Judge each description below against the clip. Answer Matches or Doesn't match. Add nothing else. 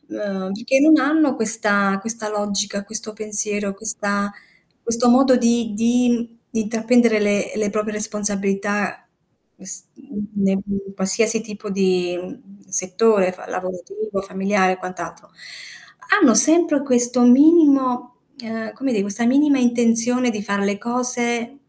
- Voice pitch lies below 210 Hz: Doesn't match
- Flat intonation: Doesn't match